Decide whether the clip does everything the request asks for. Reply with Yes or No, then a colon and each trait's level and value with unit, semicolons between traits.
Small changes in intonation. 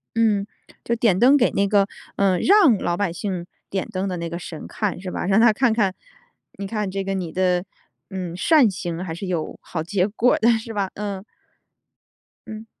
No: average, 3.3 semitones